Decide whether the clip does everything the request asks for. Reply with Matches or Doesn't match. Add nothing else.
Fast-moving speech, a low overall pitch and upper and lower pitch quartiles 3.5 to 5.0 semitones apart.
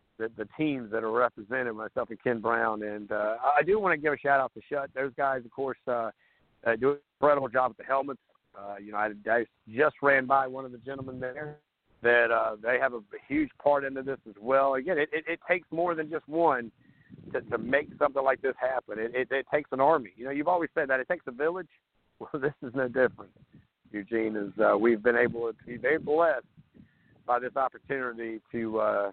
Matches